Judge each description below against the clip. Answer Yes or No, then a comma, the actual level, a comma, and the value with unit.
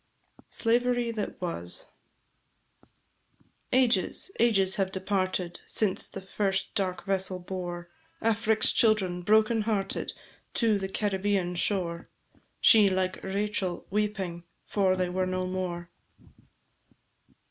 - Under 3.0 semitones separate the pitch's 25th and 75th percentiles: Yes, narrow, 2.4 semitones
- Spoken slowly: Yes, slow, 110 wpm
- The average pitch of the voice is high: Yes, high, 195 Hz